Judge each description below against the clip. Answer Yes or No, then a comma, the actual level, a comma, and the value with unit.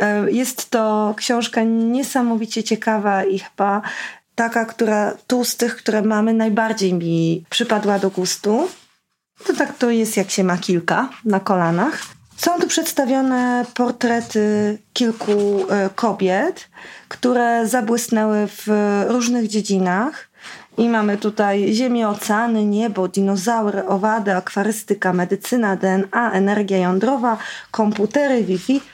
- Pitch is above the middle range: Yes, high, 215 Hz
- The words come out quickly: No, average, 115 wpm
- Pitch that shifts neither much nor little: Yes, average, 3.0 semitones